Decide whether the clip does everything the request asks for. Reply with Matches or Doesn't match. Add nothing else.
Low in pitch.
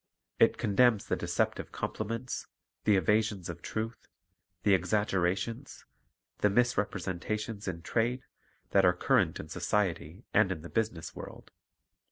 Matches